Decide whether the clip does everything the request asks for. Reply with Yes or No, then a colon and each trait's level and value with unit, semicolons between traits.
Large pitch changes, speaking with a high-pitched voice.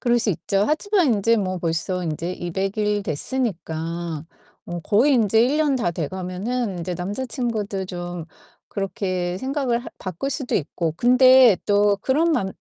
Yes: wide, 5.8 semitones; high, 200 Hz